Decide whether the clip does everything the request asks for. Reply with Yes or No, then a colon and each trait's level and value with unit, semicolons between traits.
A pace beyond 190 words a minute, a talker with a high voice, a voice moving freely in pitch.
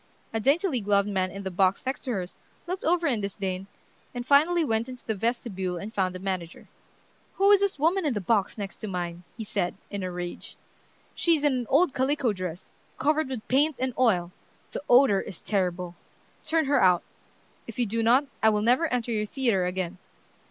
Yes: average, 200 wpm; high, 220 Hz; wide, 6.4 semitones